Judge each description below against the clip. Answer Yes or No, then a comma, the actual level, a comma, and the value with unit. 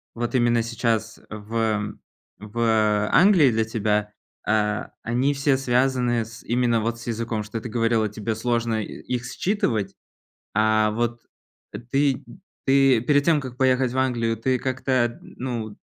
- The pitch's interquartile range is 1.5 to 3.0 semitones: Yes, average, 2.7 semitones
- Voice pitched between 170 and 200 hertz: No, low, 115 Hz